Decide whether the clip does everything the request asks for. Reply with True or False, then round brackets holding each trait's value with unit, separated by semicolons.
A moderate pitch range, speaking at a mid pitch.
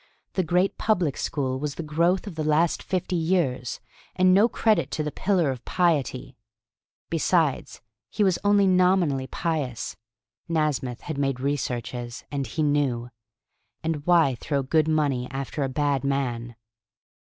True (4.6 semitones; 150 Hz)